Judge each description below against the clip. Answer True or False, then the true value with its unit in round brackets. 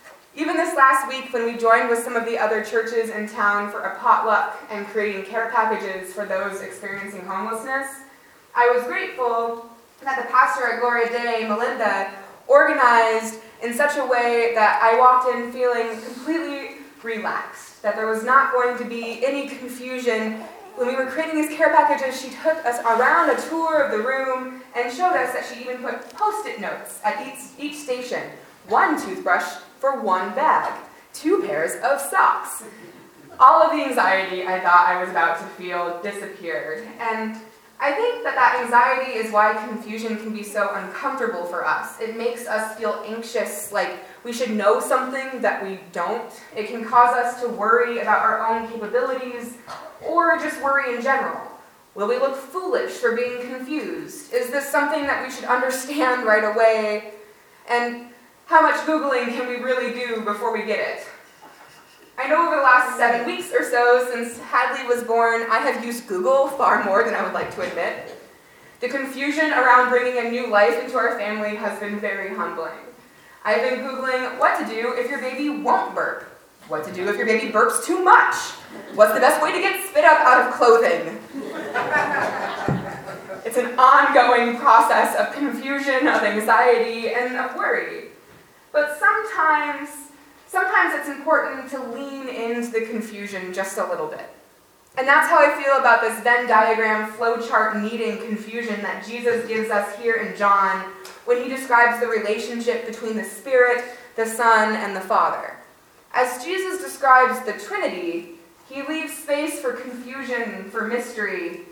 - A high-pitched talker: True (240 Hz)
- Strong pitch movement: False (3.7 semitones)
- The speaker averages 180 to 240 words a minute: False (170 wpm)